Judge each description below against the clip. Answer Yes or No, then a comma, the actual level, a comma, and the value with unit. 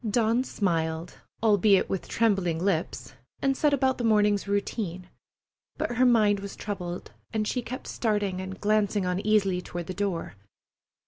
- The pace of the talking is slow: No, average, 145 wpm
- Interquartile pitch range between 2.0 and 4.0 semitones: Yes, average, 3.2 semitones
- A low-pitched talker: No, high, 205 Hz